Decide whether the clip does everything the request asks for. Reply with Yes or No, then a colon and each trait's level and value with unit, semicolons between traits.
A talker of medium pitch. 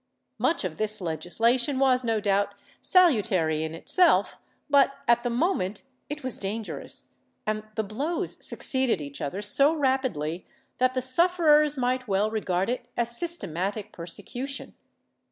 No: high, 235 Hz